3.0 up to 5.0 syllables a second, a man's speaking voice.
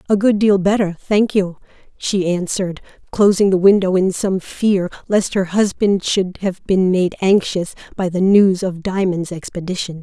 No: 4.5 syllables/s; female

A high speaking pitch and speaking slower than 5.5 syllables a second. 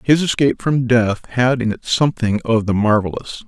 No: low, 120 Hz; 5.3 syllables/s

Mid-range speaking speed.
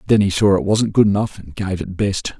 No: fast, 275 wpm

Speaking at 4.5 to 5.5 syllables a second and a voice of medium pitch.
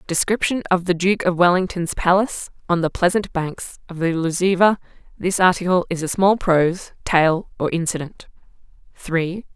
Yes: 4.9 syllables/s; medium, 175 Hz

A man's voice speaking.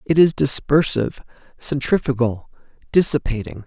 Yes: male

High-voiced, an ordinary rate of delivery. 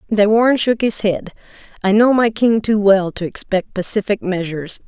Yes: high, 210 Hz; average, 185 wpm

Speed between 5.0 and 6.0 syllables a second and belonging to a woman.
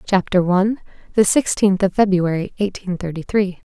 Yes: 5.1 syllables/s; female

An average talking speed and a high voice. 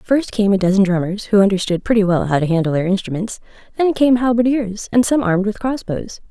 No: fast, 220 wpm; high, 205 Hz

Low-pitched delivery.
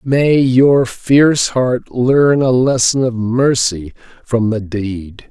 Yes: low, 125 Hz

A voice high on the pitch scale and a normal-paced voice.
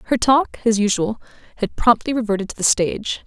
Yes: high, 220 Hz; average, 185 wpm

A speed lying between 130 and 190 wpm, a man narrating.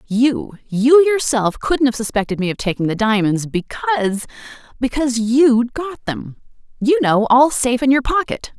No: average, 145 wpm; female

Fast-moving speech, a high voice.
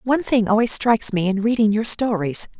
Yes: fast, 210 wpm; high, 220 Hz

